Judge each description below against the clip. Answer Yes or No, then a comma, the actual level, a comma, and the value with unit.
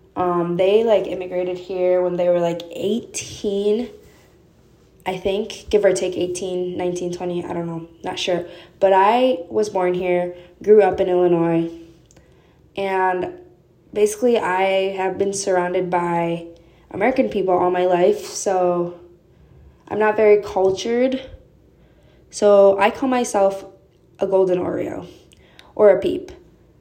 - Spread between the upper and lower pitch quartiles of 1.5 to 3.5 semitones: Yes, narrow, 2.4 semitones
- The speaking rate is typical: No, slow, 130 wpm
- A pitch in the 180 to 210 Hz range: Yes, medium, 185 Hz